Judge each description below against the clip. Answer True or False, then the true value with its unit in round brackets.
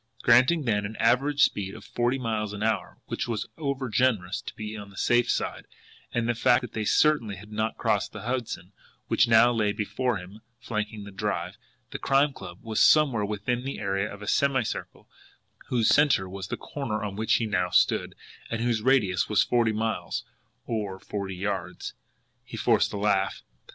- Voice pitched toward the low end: True (110 Hz)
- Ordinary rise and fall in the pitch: True (3.2 semitones)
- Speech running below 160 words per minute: False (180 wpm)